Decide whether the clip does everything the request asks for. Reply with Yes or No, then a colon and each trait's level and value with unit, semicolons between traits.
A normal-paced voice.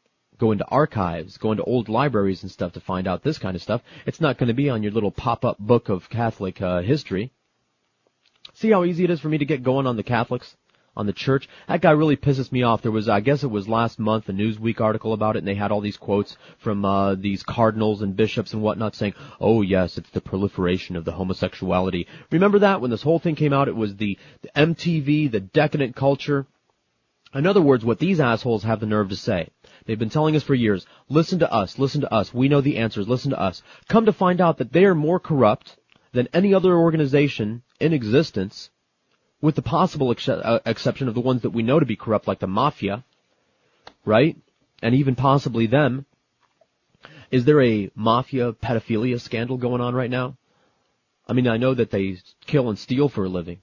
No: fast, 215 wpm